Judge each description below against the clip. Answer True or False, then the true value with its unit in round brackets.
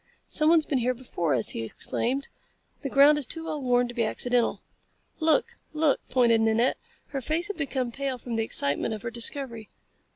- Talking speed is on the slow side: False (185 wpm)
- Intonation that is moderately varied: True (3.9 semitones)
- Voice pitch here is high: True (250 Hz)